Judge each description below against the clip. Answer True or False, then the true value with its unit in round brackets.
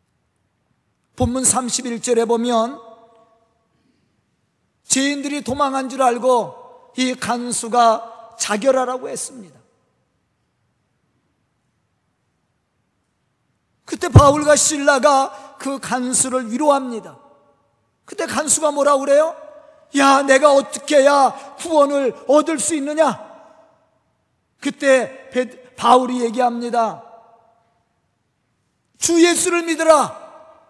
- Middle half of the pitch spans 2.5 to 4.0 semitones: True (3.7 semitones)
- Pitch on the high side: True (270 Hz)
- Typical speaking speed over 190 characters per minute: False (175 characters per minute)